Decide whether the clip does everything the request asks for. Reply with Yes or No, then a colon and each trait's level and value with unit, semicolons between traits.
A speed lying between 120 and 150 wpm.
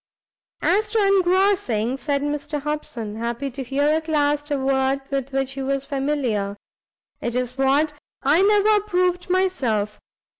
Yes: average, 140 wpm